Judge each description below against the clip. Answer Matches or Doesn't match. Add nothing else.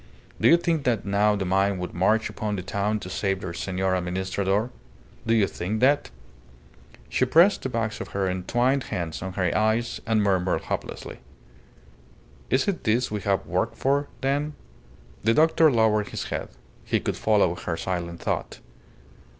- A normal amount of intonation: Matches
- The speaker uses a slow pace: Doesn't match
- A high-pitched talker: Doesn't match